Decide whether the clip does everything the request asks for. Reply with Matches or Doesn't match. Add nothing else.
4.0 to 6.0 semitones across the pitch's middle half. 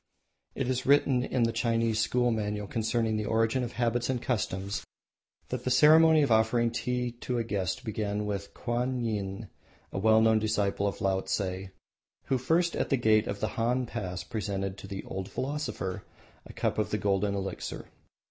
Doesn't match